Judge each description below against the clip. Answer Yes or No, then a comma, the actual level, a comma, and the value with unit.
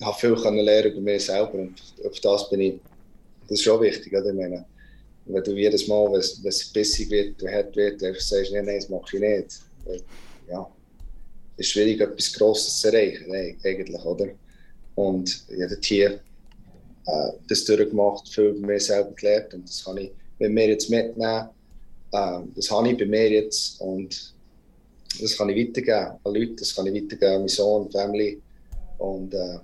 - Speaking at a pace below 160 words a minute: No, fast, 190 wpm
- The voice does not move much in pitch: Yes, narrow, 1.6 semitones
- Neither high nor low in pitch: No, low, 100 Hz